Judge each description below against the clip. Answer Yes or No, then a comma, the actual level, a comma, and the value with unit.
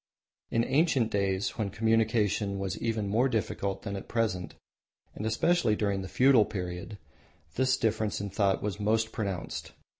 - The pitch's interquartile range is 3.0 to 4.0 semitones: No, narrow, 2.4 semitones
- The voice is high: No, low, 105 Hz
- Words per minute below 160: Yes, average, 150 wpm